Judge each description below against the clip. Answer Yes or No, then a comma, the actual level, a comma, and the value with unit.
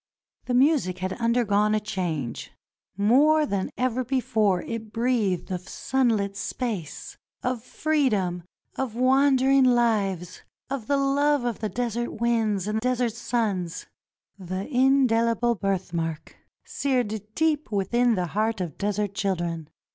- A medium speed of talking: No, slow, 130 wpm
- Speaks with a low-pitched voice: No, high, 225 Hz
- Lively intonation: No, average, 4.7 semitones